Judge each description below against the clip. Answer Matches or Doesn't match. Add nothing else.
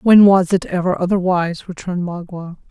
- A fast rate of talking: Doesn't match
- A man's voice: Doesn't match